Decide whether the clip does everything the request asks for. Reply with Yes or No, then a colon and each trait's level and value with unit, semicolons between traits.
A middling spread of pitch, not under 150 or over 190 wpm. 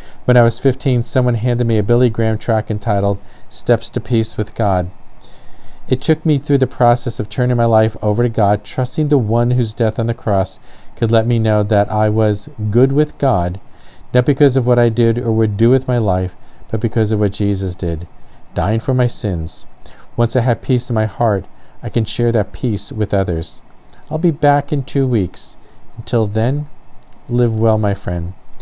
No: average, 3.0 semitones; average, 200 wpm